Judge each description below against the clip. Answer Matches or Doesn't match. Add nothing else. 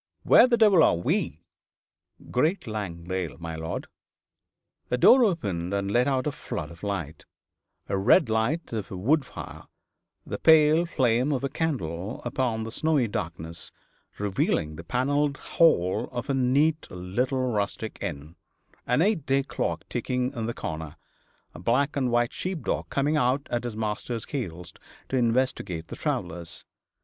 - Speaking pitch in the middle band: Doesn't match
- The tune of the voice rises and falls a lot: Matches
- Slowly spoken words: Doesn't match